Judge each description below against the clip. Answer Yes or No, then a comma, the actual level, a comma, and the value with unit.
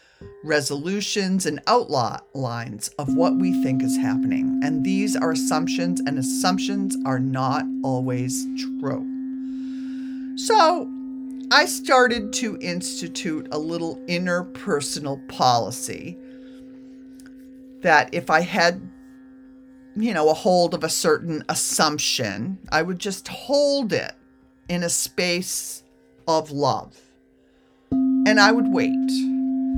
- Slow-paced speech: Yes, slow, 110 wpm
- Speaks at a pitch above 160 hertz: Yes, medium, 185 Hz